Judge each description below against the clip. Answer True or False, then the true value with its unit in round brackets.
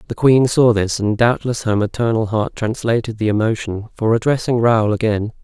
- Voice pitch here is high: False (115 Hz)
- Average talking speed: True (175 wpm)